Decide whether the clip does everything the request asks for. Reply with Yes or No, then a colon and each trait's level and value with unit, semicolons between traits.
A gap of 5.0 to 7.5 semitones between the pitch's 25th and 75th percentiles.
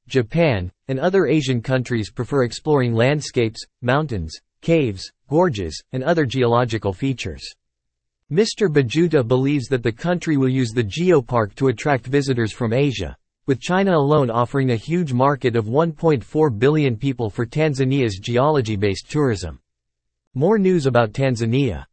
No: average, 4.5 semitones